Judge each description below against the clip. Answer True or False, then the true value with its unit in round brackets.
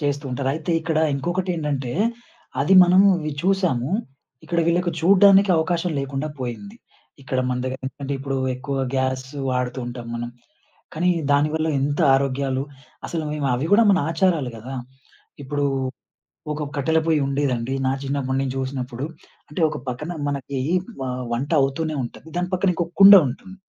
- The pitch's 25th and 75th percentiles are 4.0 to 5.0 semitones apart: True (4.3 semitones)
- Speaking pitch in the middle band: True (145 Hz)